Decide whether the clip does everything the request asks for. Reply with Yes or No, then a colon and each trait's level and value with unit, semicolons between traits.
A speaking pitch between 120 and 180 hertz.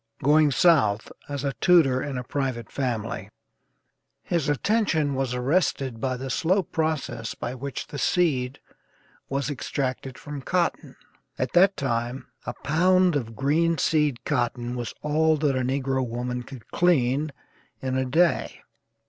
Yes: low, 135 Hz